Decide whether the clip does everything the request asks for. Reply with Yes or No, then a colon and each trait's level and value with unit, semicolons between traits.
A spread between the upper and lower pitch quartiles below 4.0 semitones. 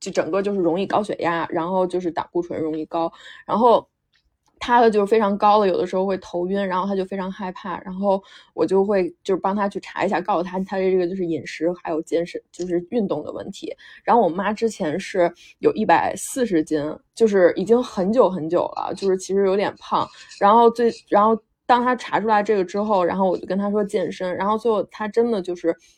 Yes: average, 2.9 semitones